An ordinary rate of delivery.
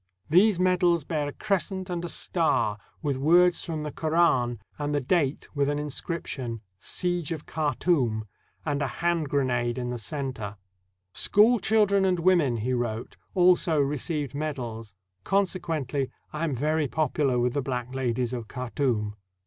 Yes: average, 160 wpm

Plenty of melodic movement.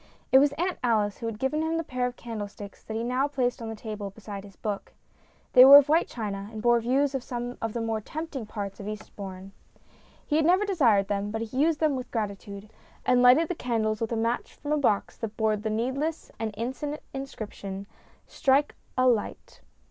No: average, 4.4 semitones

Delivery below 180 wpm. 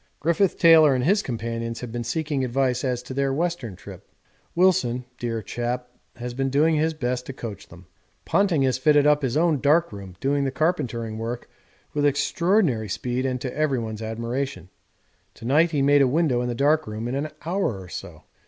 No: average, 190 wpm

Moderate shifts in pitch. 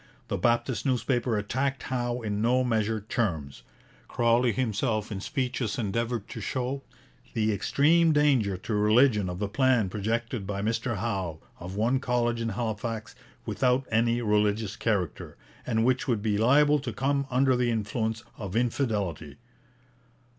Yes: average, 3.2 semitones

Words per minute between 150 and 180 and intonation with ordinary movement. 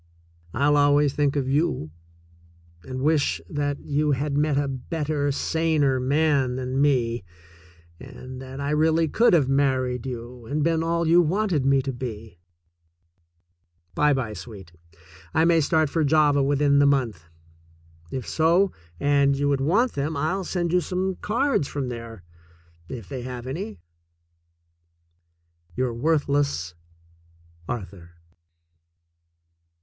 No: slow, 135 wpm; average, 3.5 semitones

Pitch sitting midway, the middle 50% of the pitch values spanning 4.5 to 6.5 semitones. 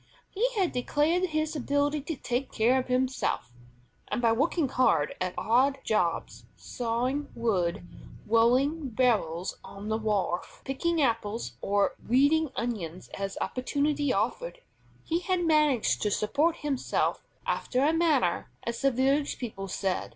No: very high, 255 Hz; wide, 5.4 semitones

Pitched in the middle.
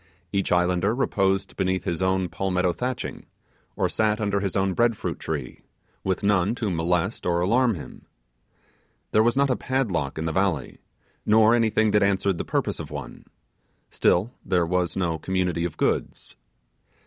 No: very low, 95 Hz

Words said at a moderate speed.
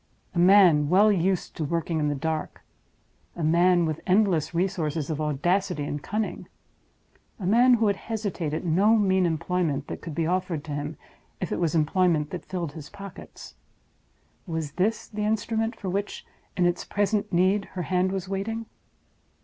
Yes: average, 165 wpm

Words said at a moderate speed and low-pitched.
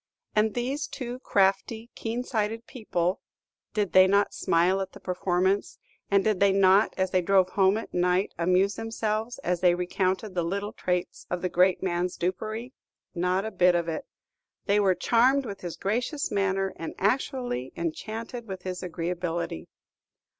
No: average, 160 wpm; high, 195 Hz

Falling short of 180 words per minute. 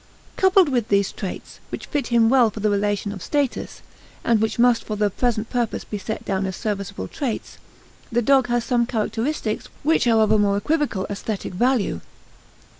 No: average, 185 wpm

